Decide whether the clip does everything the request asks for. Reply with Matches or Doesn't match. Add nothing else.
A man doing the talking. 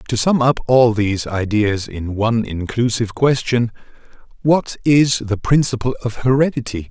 Matches